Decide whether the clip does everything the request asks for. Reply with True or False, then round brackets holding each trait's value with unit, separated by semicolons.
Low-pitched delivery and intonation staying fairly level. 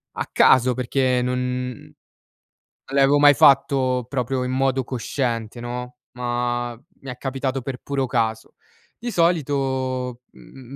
True (130 Hz; 1.6 semitones)